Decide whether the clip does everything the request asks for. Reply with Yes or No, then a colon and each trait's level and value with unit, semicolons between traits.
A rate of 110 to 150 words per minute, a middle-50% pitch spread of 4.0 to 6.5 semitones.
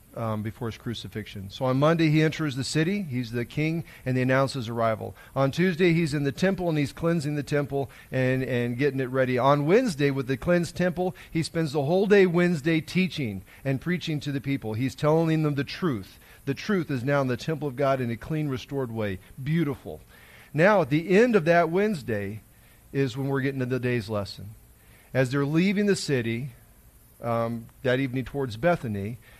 No: average, 200 wpm; average, 5.0 semitones